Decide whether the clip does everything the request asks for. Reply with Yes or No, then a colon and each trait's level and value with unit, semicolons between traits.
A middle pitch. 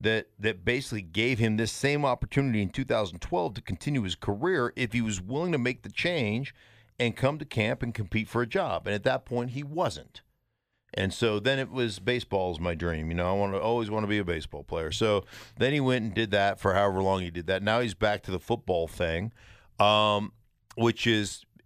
No: low, 110 Hz